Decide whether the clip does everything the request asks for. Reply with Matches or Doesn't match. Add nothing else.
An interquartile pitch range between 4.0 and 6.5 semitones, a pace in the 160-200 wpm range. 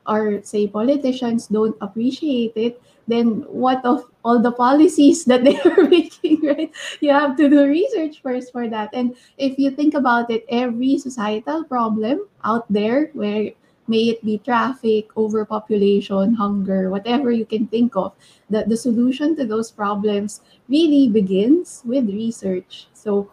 Doesn't match